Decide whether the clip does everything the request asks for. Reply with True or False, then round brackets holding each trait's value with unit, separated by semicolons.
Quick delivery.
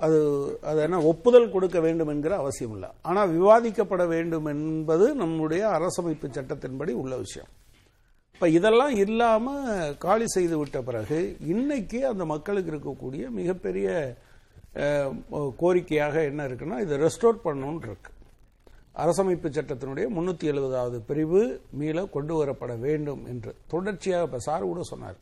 False (120 wpm)